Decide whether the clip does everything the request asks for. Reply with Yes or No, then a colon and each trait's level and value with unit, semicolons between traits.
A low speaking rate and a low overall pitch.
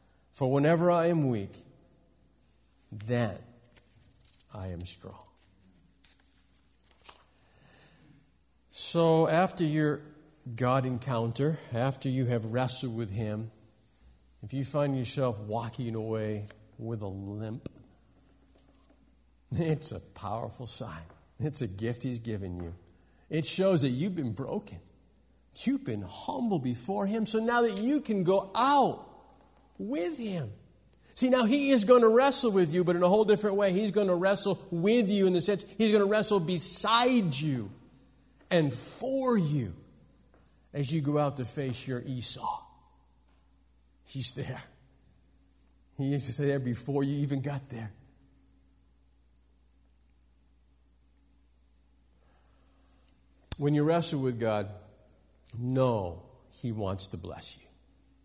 Yes: slow, 125 wpm; low, 120 Hz